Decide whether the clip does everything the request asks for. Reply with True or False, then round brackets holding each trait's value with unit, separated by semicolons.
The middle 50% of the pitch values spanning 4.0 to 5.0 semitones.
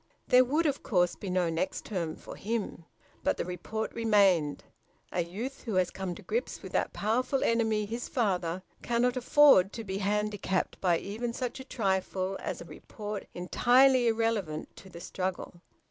True (4.4 semitones)